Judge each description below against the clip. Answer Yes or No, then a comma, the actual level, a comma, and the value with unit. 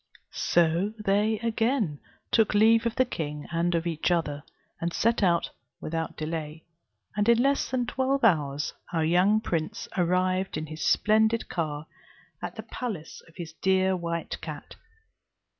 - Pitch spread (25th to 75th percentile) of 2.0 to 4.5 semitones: No, average, 5.2 semitones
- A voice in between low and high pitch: Yes, medium, 180 Hz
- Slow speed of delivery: No, average, 150 wpm